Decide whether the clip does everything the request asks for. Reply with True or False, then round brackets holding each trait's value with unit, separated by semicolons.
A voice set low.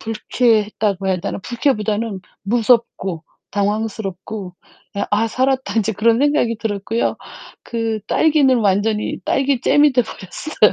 False (220 Hz)